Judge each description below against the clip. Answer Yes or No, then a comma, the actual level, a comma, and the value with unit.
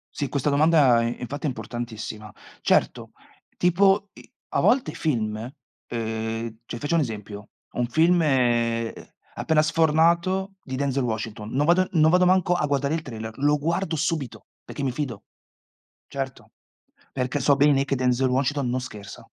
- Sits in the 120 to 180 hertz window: Yes, low, 135 Hz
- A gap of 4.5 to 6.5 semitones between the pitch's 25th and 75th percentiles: Yes, average, 5.2 semitones